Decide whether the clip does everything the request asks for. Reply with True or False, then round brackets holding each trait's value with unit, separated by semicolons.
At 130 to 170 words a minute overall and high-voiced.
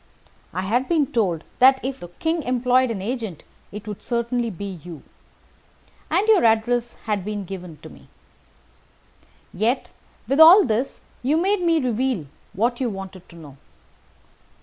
True (150 wpm; 235 Hz)